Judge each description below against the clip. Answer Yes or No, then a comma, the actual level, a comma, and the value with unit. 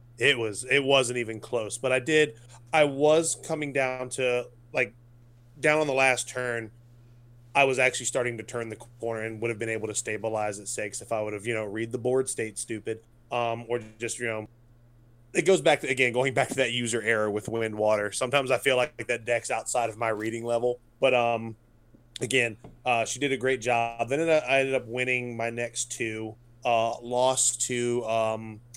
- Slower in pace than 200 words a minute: No, fast, 205 wpm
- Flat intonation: Yes, narrow, 2.0 semitones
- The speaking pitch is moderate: No, low, 120 Hz